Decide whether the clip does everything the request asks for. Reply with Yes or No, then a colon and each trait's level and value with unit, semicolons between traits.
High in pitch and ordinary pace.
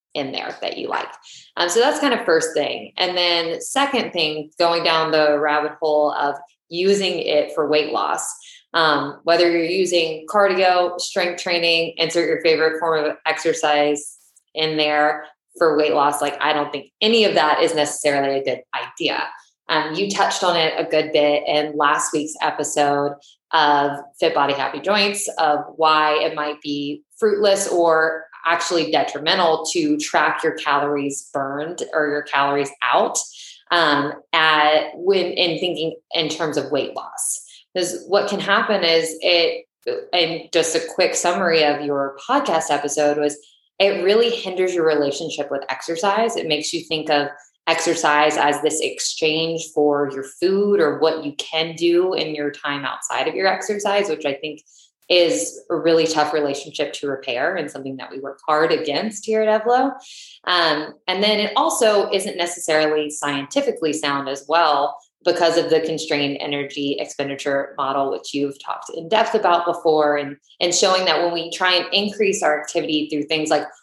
No: medium, 160 Hz; average, 170 wpm